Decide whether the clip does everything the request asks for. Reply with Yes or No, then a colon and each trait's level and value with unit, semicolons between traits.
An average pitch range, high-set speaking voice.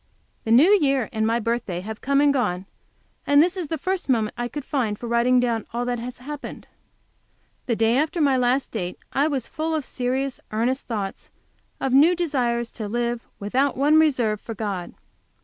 Yes: average, 3.9 semitones; high, 245 Hz